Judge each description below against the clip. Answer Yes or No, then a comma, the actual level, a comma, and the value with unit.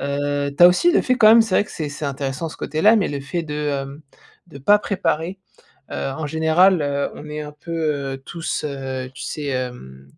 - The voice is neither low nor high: Yes, medium, 150 Hz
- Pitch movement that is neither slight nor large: Yes, average, 3.6 semitones